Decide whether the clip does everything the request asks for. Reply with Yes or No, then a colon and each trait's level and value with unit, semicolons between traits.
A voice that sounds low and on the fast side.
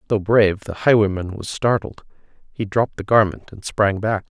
No: low, 105 Hz; average, 180 wpm